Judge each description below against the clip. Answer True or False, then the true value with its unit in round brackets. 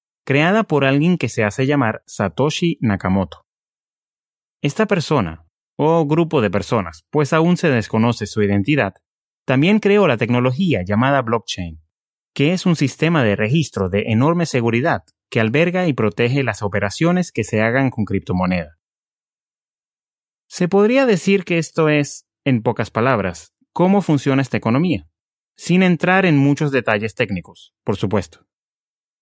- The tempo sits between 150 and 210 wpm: False (140 wpm)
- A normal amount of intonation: False (7.3 semitones)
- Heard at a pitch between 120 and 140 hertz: True (135 Hz)